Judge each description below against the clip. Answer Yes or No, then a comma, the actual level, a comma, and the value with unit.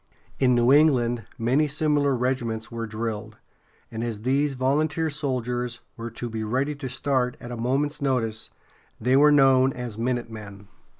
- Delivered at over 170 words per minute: No, average, 155 wpm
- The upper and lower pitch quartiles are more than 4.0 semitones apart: No, average, 3.2 semitones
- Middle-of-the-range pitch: No, low, 125 Hz